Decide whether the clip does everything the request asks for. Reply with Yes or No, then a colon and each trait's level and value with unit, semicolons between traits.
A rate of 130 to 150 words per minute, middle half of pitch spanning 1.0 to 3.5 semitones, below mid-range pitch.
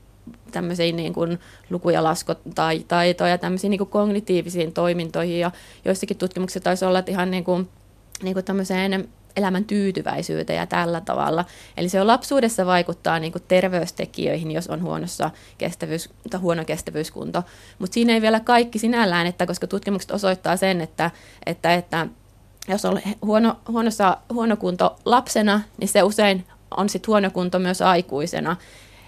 No: average, 140 wpm; average, 2.7 semitones; medium, 185 Hz